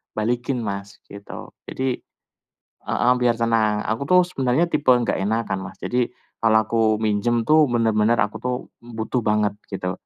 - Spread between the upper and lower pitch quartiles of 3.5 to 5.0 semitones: No, narrow, 2.6 semitones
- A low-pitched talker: Yes, low, 115 Hz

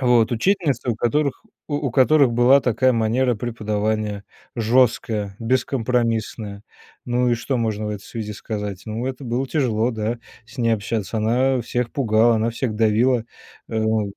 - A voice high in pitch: No, low, 115 Hz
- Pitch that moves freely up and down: No, narrow, 2.6 semitones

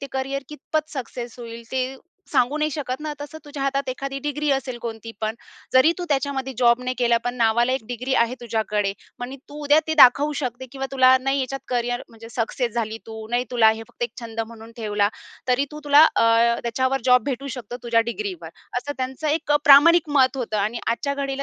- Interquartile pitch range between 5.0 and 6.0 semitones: No, average, 3.1 semitones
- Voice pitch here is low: No, very high, 255 Hz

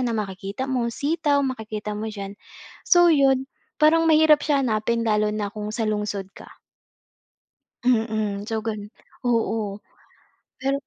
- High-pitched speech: Yes, high, 225 Hz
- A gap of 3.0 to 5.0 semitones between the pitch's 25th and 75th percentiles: Yes, average, 4.4 semitones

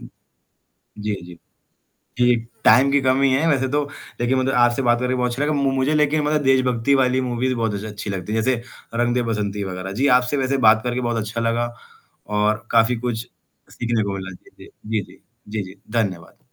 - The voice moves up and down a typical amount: Yes, average, 3.5 semitones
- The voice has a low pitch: Yes, low, 120 Hz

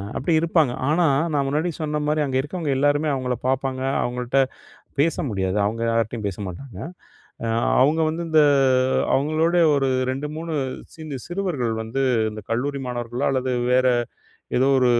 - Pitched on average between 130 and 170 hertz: Yes, low, 135 Hz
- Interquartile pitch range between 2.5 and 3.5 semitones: No, average, 4.0 semitones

